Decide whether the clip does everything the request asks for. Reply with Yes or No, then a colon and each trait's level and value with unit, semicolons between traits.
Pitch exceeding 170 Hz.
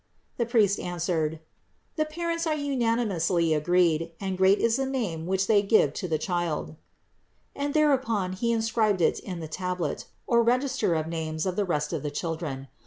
Yes: medium, 185 Hz